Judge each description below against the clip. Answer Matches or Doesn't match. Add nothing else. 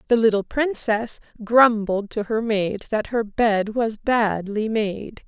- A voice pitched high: Matches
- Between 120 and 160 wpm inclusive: Matches